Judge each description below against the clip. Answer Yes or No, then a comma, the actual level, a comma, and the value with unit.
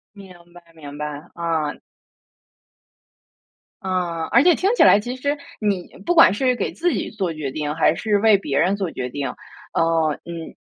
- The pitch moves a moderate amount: No, wide, 5.7 semitones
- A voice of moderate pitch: Yes, medium, 180 Hz